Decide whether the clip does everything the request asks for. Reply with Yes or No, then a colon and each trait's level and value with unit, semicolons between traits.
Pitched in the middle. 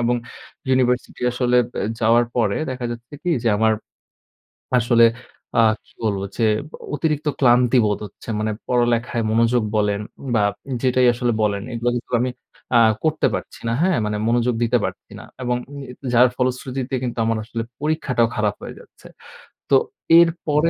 No: low, 120 Hz